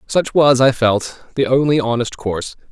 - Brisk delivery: No, average, 175 wpm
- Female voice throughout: No, male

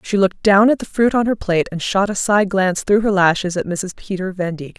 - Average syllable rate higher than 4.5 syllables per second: Yes, 6.0 syllables/s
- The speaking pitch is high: Yes, high, 195 Hz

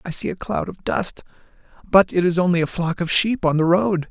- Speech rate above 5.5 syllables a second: No, 5.3 syllables/s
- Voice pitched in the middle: Yes, medium, 165 Hz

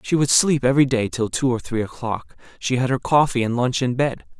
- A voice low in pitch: Yes, low, 125 Hz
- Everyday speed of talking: No, fast, 245 wpm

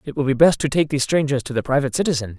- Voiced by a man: Yes, male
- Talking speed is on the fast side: Yes, fast, 300 wpm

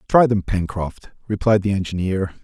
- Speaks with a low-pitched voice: Yes, low, 100 Hz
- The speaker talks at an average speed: Yes, average, 150 wpm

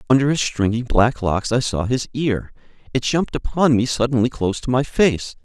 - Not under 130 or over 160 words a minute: No, average, 200 wpm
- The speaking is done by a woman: No, male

